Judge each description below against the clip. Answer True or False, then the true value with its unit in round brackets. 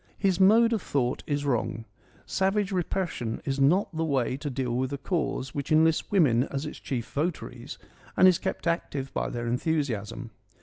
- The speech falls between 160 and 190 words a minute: True (175 wpm)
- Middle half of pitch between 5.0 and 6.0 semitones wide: True (5.3 semitones)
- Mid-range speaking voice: True (145 Hz)